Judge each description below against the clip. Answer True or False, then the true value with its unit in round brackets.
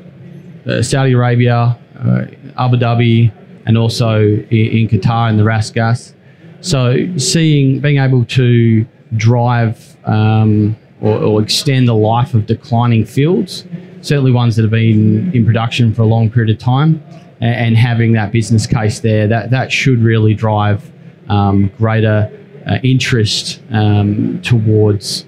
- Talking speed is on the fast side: False (140 wpm)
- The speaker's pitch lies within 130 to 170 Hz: False (115 Hz)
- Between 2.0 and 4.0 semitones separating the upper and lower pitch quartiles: True (3.7 semitones)